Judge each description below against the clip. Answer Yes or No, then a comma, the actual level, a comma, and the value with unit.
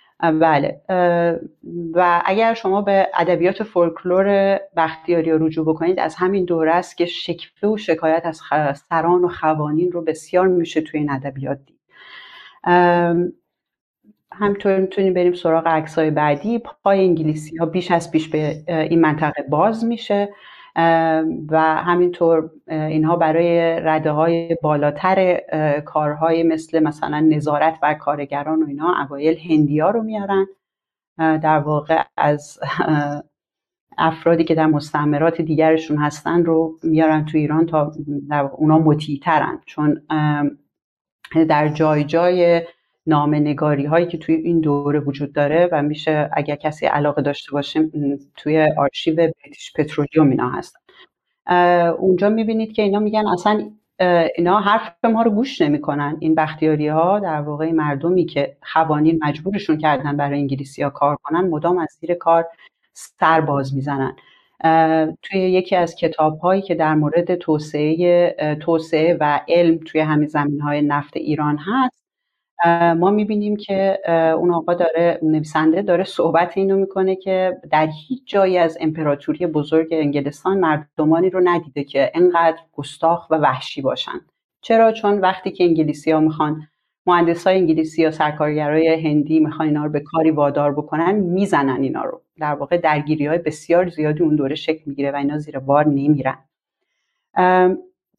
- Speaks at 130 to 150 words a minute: Yes, average, 140 wpm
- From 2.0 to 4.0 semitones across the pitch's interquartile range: Yes, average, 2.7 semitones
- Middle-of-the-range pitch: Yes, medium, 160 Hz